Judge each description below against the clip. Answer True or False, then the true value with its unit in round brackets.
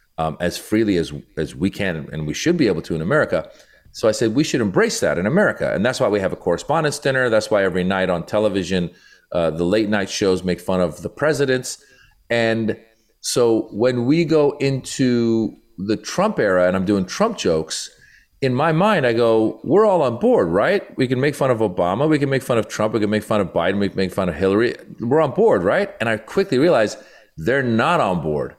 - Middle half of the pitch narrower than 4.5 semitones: False (5.3 semitones)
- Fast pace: True (225 wpm)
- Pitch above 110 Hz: False (105 Hz)